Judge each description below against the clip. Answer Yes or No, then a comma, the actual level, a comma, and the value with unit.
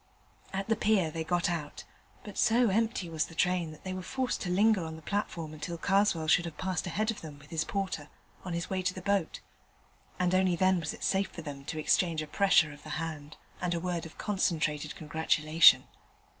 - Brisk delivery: Yes, fast, 215 wpm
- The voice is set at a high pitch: No, medium, 175 Hz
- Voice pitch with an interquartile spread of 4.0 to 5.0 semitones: No, average, 3.4 semitones